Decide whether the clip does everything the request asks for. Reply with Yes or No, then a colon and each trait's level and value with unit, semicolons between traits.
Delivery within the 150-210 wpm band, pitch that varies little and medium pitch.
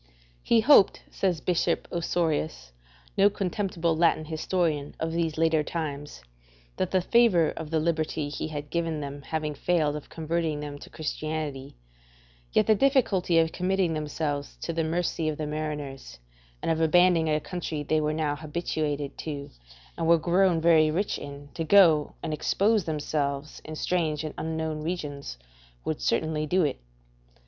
Yes: average, 155 wpm; narrow, 2.2 semitones; medium, 160 Hz